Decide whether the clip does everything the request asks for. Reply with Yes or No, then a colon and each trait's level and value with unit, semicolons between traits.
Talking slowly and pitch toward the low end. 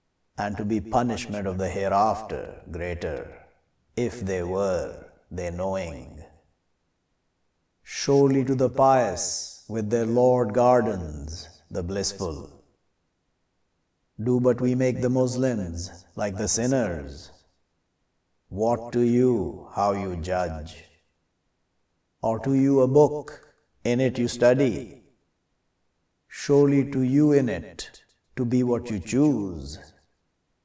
Yes: slow, 110 wpm; low, 100 Hz